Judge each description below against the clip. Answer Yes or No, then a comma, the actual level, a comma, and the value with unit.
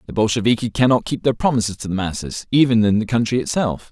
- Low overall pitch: Yes, low, 115 Hz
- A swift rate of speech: Yes, fast, 215 wpm